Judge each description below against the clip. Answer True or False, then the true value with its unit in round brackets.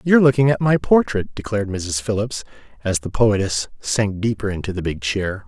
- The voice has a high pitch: False (110 Hz)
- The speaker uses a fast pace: False (185 wpm)